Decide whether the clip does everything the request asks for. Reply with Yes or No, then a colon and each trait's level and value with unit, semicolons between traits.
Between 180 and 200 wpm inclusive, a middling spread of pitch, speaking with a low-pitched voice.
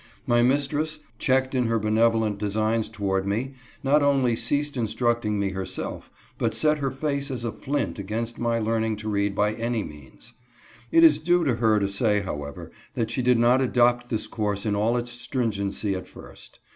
Yes: average, 185 wpm; average, 3.7 semitones; low, 115 Hz